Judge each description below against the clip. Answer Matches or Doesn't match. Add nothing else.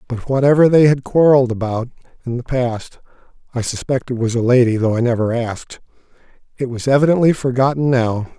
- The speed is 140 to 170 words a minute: Matches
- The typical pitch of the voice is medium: Doesn't match